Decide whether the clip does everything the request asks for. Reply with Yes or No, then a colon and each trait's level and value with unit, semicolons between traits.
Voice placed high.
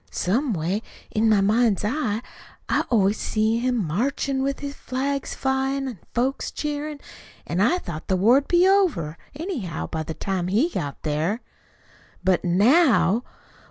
Yes: high, 230 Hz